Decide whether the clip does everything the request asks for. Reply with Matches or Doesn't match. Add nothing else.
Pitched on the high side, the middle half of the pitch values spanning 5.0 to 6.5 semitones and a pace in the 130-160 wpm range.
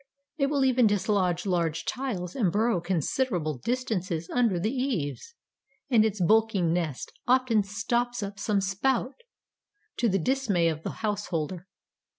Matches